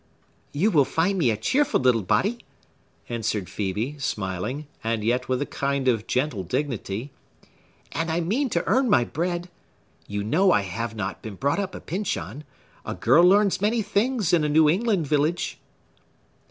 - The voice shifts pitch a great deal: Yes, wide, 8.1 semitones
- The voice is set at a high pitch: No, medium, 145 Hz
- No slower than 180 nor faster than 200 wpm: No, average, 165 wpm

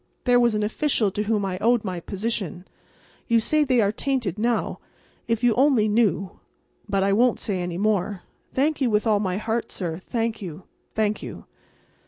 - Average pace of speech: Yes, average, 170 wpm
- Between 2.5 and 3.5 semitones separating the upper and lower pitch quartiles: Yes, average, 3.2 semitones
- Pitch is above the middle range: Yes, high, 215 Hz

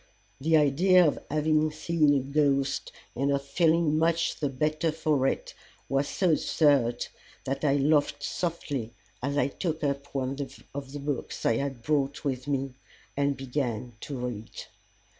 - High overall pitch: No, medium, 140 Hz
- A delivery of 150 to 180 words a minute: Yes, average, 155 wpm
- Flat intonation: Yes, narrow, 2.2 semitones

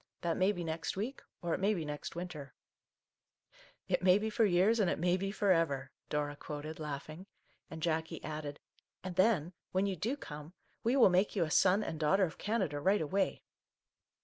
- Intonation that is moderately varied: Yes, average, 4.2 semitones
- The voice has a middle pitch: Yes, medium, 175 Hz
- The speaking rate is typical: No, fast, 215 wpm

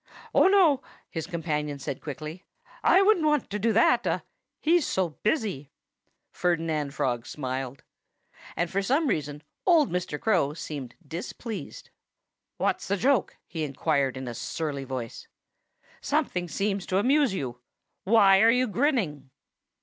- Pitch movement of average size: No, wide, 8.0 semitones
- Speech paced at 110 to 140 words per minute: Yes, slow, 135 wpm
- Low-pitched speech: No, medium, 175 Hz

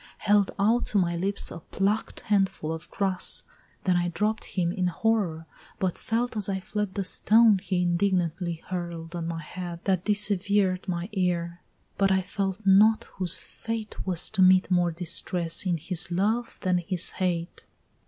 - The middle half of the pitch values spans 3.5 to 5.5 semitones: No, narrow, 2.6 semitones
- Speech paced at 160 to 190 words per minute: Yes, average, 165 wpm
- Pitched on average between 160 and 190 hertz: Yes, medium, 185 Hz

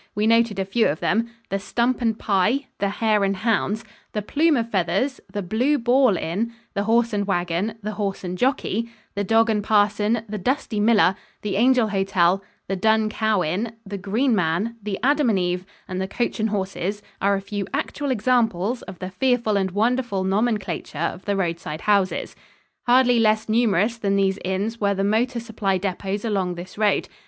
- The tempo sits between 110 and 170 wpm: No, average, 185 wpm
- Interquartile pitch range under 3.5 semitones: Yes, average, 3.1 semitones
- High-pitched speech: Yes, high, 210 Hz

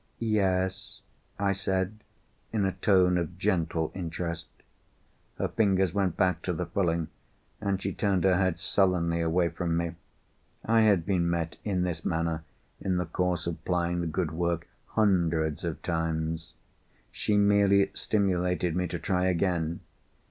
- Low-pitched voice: Yes, very low, 90 Hz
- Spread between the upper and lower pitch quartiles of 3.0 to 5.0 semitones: No, narrow, 2.4 semitones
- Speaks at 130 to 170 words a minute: Yes, average, 150 wpm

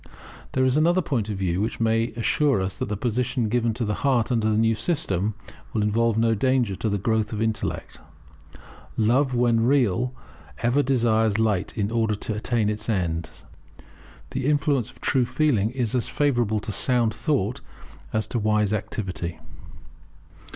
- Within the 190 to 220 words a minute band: No, average, 165 wpm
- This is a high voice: No, low, 115 Hz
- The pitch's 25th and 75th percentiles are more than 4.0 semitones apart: No, average, 3.0 semitones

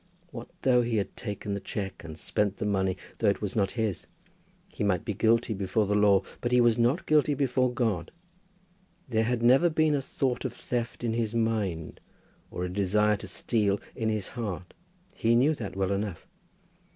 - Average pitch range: Yes, average, 3.4 semitones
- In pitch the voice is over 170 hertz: No, low, 110 Hz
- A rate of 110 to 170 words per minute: No, average, 190 wpm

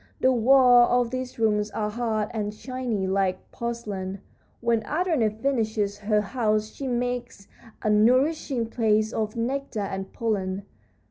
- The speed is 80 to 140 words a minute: Yes, slow, 135 wpm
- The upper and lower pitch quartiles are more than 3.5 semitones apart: No, average, 2.9 semitones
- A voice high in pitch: Yes, high, 225 Hz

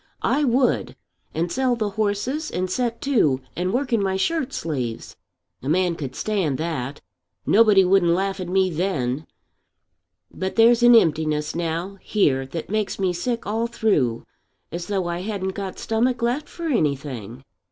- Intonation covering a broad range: Yes, wide, 6.2 semitones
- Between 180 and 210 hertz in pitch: Yes, high, 190 Hz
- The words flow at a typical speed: Yes, average, 160 wpm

